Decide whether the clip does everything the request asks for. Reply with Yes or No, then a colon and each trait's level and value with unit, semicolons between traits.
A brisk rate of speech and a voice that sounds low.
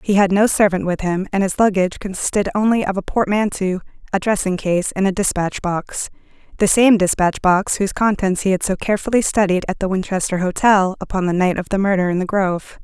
No: fast, 210 wpm; high, 195 Hz